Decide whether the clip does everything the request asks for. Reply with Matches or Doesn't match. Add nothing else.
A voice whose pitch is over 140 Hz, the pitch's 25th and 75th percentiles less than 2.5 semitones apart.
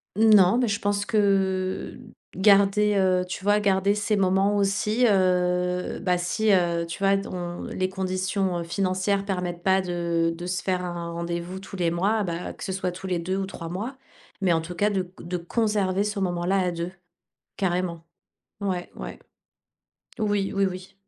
Matches